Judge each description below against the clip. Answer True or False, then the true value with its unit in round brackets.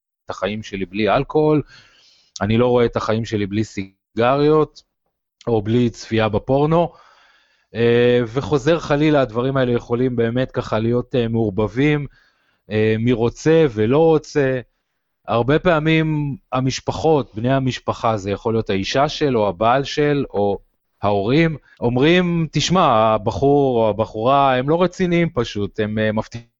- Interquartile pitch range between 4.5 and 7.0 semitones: True (4.9 semitones)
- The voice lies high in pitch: False (120 Hz)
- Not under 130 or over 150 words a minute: False (120 wpm)